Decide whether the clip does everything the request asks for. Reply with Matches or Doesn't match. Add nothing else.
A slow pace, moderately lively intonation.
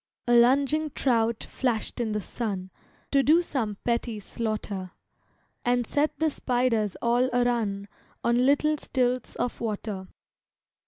Matches